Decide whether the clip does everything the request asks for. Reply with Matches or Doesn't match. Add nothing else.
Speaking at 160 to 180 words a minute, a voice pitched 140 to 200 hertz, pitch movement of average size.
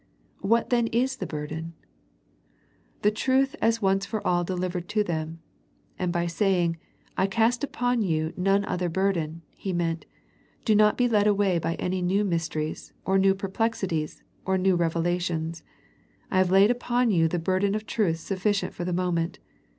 Matches